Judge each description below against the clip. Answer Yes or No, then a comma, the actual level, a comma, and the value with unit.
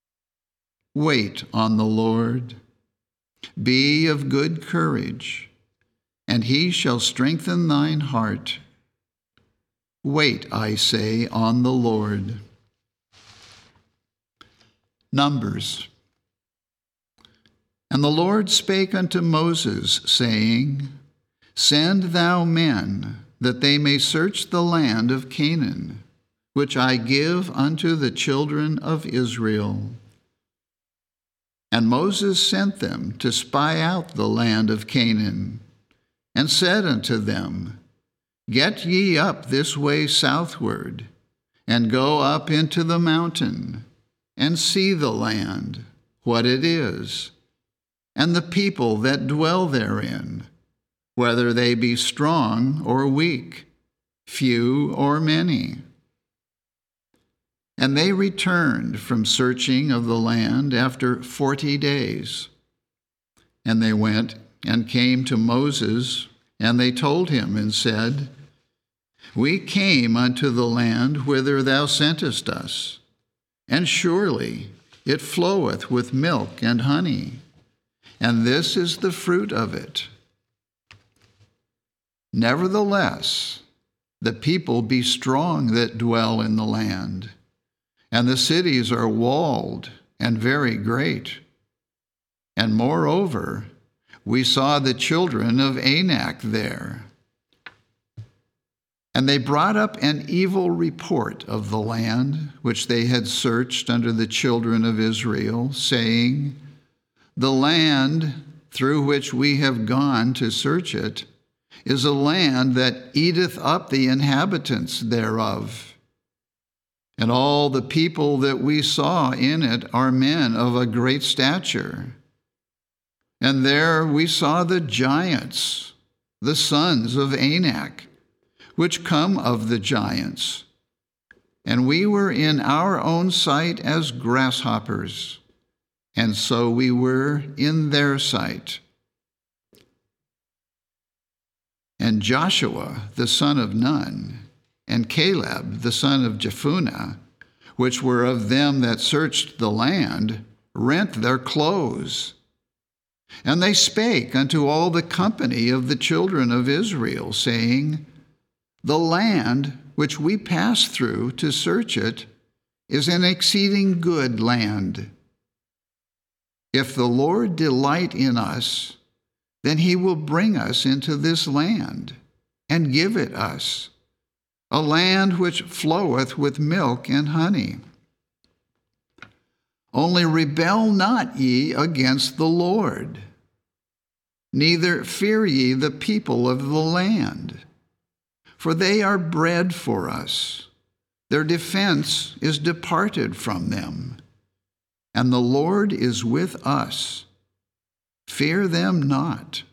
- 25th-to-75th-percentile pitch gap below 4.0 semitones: No, average, 5.3 semitones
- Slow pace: Yes, slow, 110 wpm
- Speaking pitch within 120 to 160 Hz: Yes, low, 130 Hz